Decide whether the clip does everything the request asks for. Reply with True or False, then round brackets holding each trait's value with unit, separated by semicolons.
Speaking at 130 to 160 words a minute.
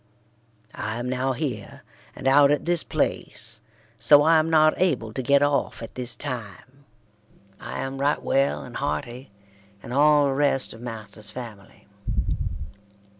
True (150 wpm)